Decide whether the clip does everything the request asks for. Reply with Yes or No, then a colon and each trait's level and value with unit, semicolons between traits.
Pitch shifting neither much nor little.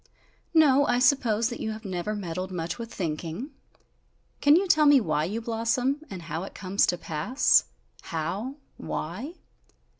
No: wide, 6.9 semitones